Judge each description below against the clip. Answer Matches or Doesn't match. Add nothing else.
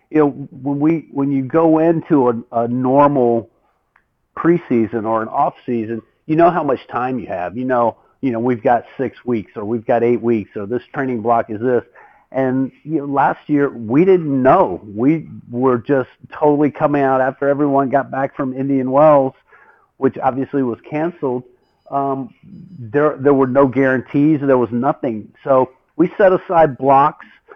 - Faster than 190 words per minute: Doesn't match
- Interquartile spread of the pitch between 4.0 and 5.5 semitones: Doesn't match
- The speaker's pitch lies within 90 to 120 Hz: Doesn't match